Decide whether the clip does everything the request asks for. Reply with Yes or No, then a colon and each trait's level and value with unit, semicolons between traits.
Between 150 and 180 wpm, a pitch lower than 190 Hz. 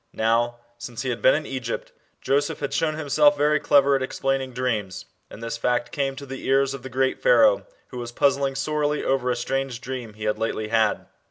No: fast, 205 wpm; low, 135 Hz